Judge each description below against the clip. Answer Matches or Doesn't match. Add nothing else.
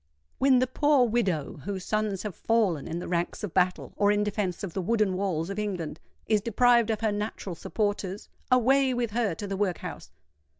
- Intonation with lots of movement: Doesn't match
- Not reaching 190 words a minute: Doesn't match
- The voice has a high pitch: Matches